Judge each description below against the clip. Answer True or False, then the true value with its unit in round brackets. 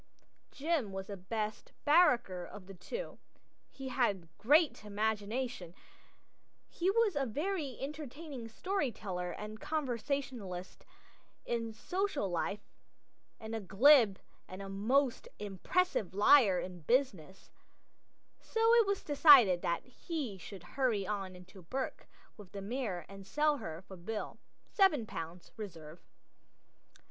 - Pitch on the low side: False (220 Hz)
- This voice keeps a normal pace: False (125 wpm)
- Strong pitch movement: True (6.7 semitones)